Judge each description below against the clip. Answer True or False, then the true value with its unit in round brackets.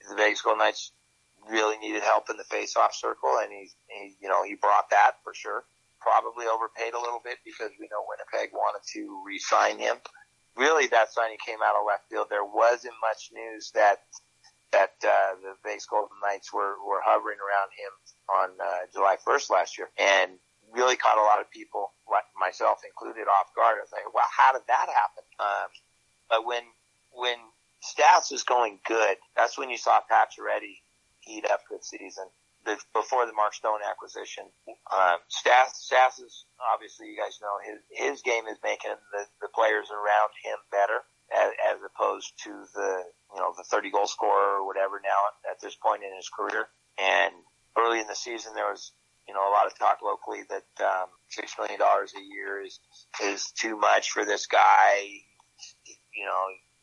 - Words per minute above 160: True (185 wpm)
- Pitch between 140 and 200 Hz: False (110 Hz)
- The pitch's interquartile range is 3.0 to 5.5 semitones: True (3.7 semitones)